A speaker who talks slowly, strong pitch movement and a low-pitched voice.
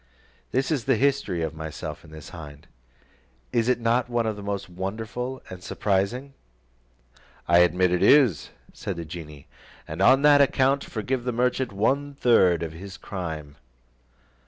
No: average, 155 wpm; wide, 6.7 semitones; low, 100 Hz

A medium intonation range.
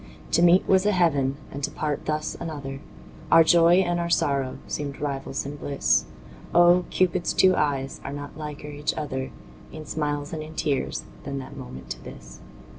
Yes: average, 3.5 semitones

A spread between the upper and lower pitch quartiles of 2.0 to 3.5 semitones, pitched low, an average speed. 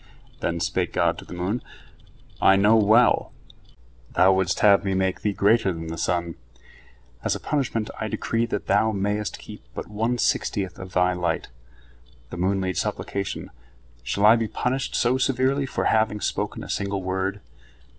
Yes: average, 3.1 semitones; low, 100 Hz; average, 165 wpm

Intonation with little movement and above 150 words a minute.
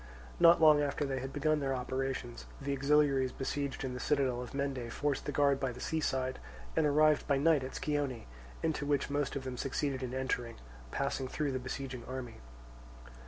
Yes: narrow, 1.9 semitones; average, 190 wpm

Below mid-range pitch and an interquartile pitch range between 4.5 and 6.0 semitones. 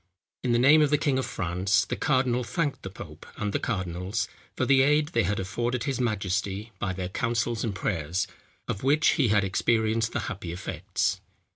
Yes: low, 110 Hz; average, 5.2 semitones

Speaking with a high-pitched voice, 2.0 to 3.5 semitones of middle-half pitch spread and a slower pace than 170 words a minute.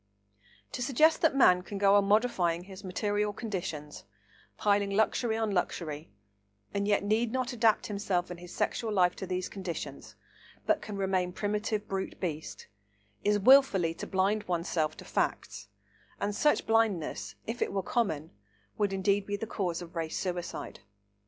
Yes: high, 200 Hz; average, 3.2 semitones; average, 160 wpm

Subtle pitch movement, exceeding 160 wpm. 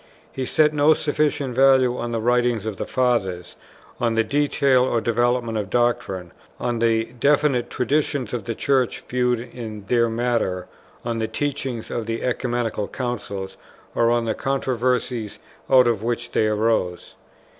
No: narrow, 2.2 semitones; average, 155 wpm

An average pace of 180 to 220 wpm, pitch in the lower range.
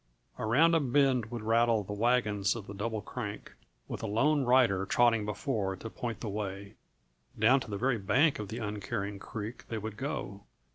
Yes: average, 185 wpm; low, 110 Hz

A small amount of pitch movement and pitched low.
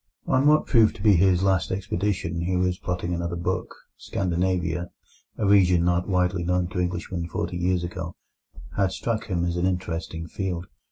Yes: narrow, 1.6 semitones; very low, 90 Hz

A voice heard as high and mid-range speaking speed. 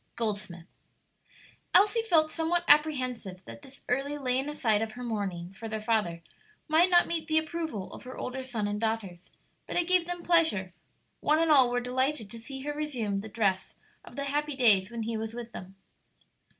Yes: high, 245 Hz; average, 190 wpm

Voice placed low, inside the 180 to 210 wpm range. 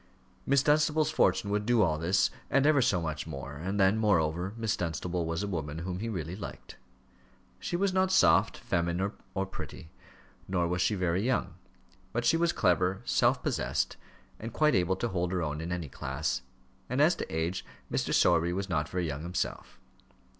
Yes: very low, 90 Hz; average, 185 wpm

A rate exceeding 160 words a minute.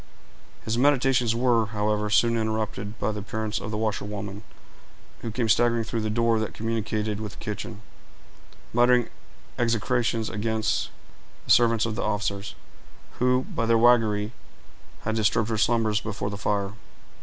No: average, 145 wpm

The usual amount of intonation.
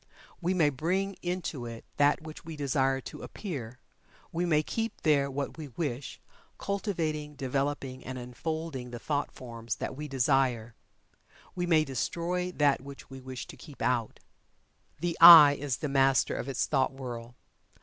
Yes: average, 3.7 semitones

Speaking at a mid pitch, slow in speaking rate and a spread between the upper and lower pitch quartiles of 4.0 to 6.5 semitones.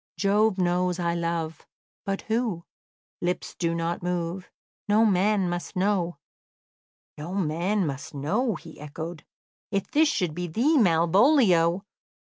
No: medium, 180 Hz; slow, 125 wpm; average, 3.5 semitones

